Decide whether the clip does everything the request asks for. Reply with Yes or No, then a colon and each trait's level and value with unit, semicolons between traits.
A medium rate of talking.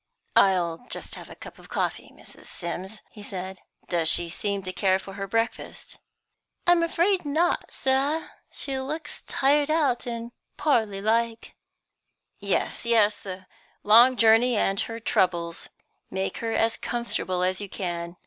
Yes: average, 150 wpm